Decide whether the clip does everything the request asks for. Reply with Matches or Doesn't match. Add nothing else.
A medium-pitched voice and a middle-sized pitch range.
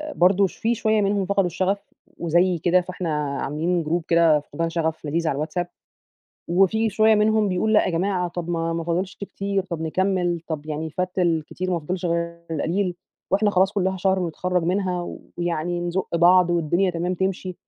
Doesn't match